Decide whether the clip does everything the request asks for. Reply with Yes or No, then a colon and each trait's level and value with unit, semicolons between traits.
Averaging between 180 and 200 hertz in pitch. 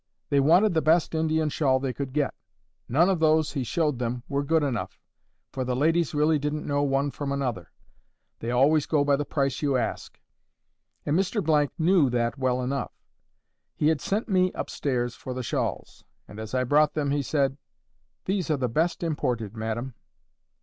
No: medium, 145 Hz